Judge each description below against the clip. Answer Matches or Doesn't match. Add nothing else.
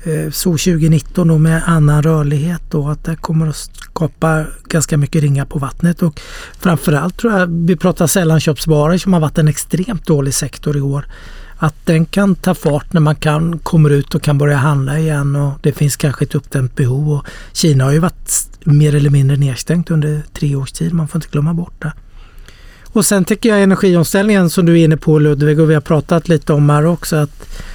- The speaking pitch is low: Doesn't match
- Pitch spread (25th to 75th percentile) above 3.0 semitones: Doesn't match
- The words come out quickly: Matches